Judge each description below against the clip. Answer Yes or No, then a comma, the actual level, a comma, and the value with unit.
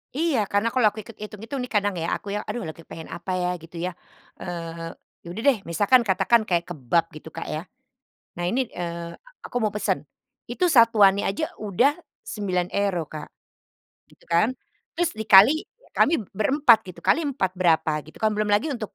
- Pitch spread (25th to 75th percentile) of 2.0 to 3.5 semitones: No, average, 5.1 semitones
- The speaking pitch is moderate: No, high, 200 Hz